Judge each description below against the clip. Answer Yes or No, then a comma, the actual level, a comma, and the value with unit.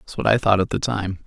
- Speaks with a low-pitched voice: Yes, low, 100 Hz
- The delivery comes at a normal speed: No, fast, 380 wpm